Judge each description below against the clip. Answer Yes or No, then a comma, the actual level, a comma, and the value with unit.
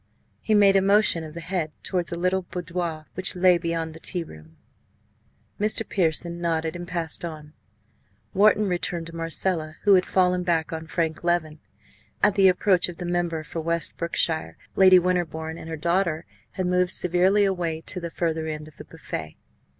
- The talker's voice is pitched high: No, medium, 170 Hz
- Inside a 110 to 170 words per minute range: No, average, 180 wpm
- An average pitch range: No, narrow, 2.2 semitones